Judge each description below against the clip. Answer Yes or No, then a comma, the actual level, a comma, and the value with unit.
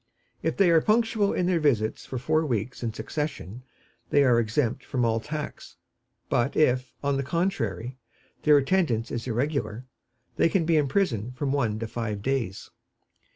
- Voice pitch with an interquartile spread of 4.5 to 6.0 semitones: Yes, average, 5.3 semitones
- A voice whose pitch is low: Yes, low, 130 Hz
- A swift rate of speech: No, average, 160 wpm